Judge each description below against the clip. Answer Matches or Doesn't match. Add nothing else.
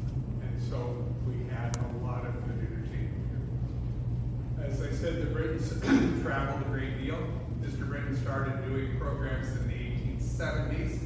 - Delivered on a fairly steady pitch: Matches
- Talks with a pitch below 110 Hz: Doesn't match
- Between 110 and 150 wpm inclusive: Matches